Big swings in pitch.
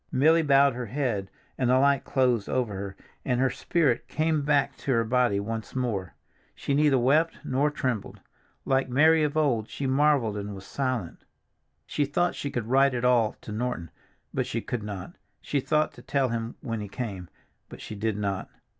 No: average, 4.3 semitones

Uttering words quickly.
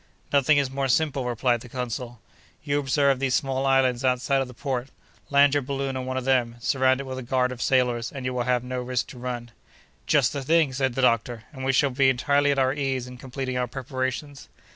Yes: fast, 230 wpm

